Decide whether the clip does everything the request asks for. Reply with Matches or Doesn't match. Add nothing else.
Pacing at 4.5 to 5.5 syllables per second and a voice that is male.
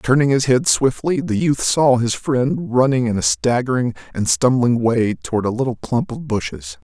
Matches